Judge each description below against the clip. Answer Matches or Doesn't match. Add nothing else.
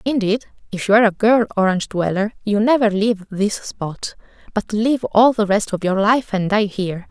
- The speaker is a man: Doesn't match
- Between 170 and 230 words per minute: Matches